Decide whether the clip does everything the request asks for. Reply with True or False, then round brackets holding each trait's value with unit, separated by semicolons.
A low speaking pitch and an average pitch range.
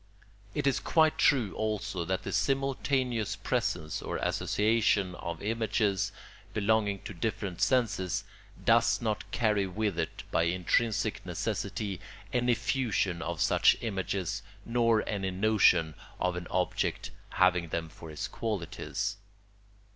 True (105 Hz; 3.9 semitones)